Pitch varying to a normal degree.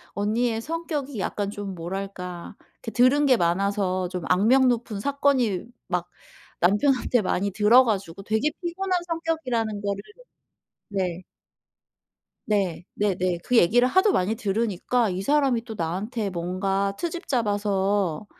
Yes: average, 4.8 semitones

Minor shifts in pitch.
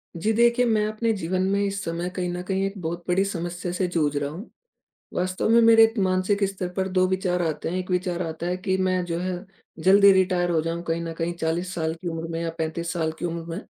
Yes: narrow, 2.2 semitones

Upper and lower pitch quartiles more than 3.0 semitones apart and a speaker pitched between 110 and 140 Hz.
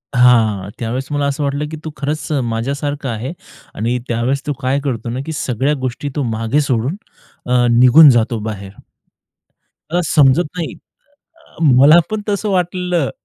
Yes: average, 4.0 semitones; low, 135 Hz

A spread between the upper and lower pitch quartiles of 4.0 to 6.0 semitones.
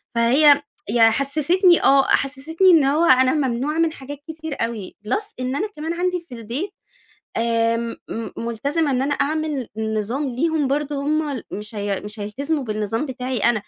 Yes: average, 4.9 semitones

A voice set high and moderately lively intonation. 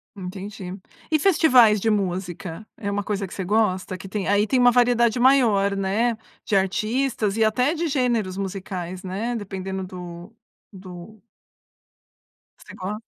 Yes: high, 205 Hz; average, 3.7 semitones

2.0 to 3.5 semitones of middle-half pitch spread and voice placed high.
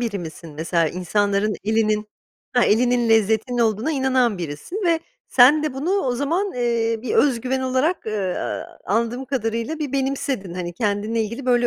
No: average, 4.0 semitones; high, 235 Hz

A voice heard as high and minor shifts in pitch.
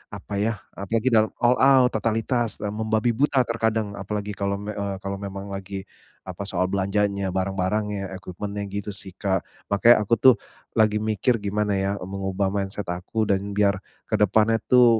No: low, 105 Hz; narrow, 2.1 semitones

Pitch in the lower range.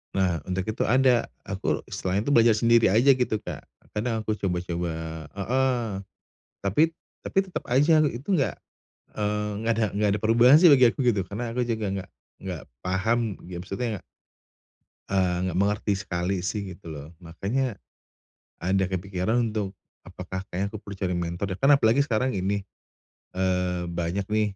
Yes: low, 100 Hz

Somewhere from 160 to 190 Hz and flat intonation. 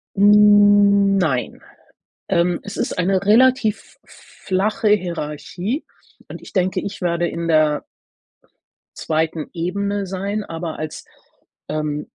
No: medium, 185 Hz; average, 3.7 semitones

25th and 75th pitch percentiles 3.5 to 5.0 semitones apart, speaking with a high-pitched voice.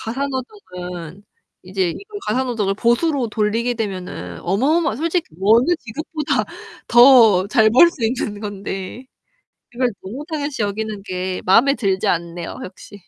No: wide, 5.5 semitones; high, 220 Hz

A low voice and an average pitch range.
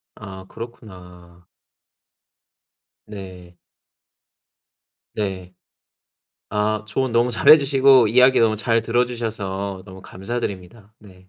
Yes: low, 105 Hz; average, 3.9 semitones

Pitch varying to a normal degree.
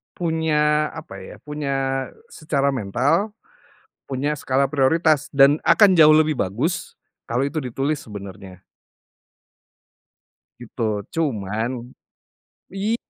Yes: average, 3.7 semitones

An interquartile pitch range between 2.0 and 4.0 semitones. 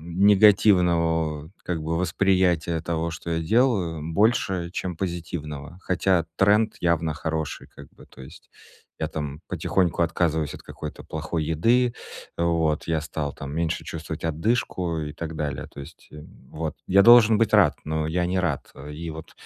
Yes: average, 2.9 semitones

